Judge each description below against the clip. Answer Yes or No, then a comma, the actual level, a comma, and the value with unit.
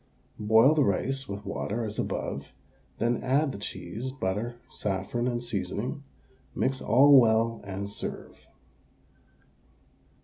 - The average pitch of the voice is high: No, low, 115 Hz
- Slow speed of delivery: Yes, slow, 115 wpm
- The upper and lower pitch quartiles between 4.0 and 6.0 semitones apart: Yes, average, 4.3 semitones